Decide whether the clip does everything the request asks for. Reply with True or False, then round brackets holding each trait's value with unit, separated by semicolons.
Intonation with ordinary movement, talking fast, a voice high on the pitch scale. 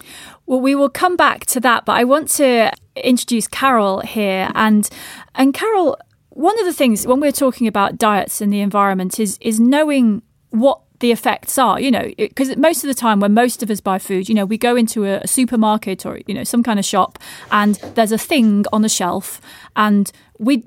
True (4.2 semitones; 210 wpm; 230 Hz)